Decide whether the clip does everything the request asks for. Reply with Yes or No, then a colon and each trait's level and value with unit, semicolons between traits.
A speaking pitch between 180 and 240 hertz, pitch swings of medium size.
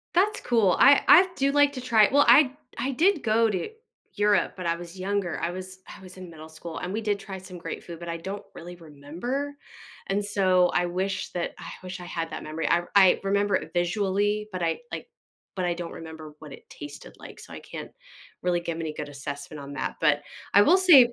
Yes: medium, 185 Hz; average, 4.0 semitones